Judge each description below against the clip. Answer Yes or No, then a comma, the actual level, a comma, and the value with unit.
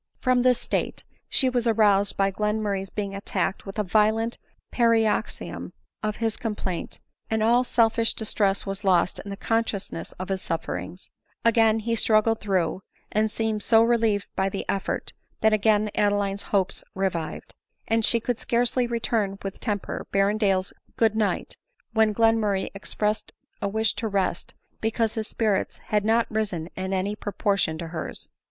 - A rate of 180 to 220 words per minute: No, average, 155 wpm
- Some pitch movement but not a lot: No, narrow, 2.3 semitones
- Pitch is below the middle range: No, high, 210 Hz